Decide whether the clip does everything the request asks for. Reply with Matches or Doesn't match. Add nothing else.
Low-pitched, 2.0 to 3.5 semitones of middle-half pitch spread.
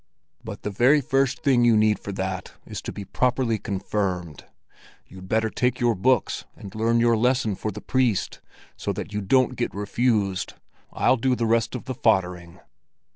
Doesn't match